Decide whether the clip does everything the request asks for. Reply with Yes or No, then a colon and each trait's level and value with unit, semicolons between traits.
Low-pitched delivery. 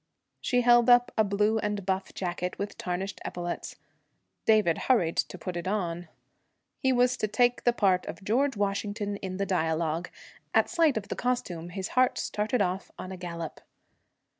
No: high, 200 Hz